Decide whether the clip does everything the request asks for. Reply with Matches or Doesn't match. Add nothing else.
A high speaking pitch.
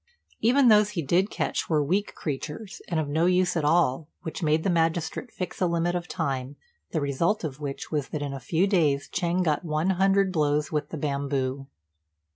Doesn't match